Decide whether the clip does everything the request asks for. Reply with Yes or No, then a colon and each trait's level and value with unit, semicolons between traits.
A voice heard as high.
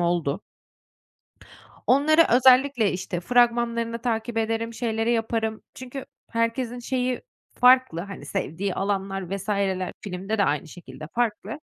Yes: high, 225 Hz